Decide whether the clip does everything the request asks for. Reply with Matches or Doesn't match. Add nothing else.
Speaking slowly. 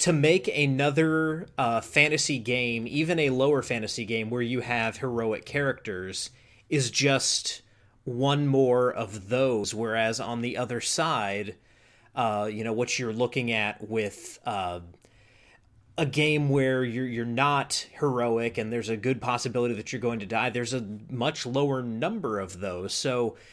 Doesn't match